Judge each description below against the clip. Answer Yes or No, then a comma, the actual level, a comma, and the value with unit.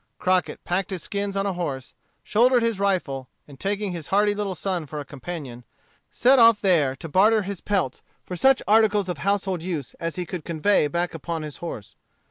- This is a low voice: No, medium, 185 Hz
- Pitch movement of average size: Yes, average, 4.5 semitones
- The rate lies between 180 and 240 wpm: Yes, average, 195 wpm